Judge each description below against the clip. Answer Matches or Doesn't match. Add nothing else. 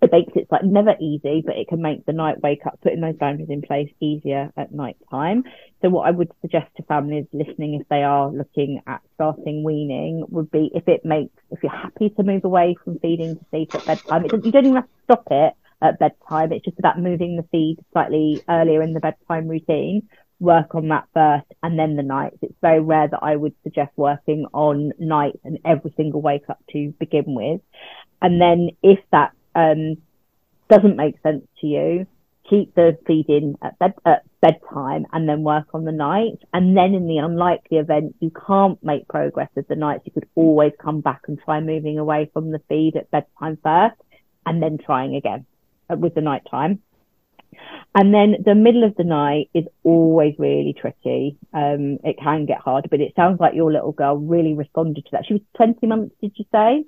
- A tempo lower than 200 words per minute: Doesn't match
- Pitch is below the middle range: Doesn't match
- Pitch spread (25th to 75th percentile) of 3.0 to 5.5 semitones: Doesn't match